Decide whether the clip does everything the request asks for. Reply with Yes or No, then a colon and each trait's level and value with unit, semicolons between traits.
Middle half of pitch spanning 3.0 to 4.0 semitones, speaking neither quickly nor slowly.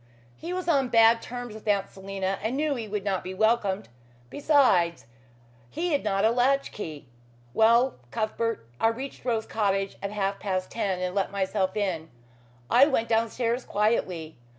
Yes: average, 3.7 semitones; average, 165 wpm